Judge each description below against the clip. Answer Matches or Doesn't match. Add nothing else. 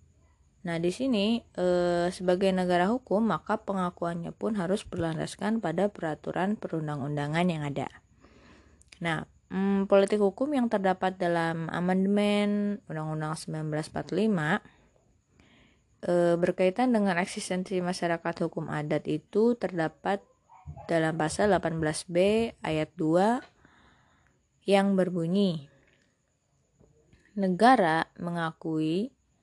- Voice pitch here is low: Doesn't match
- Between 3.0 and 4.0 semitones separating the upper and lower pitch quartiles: Matches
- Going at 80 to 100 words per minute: Matches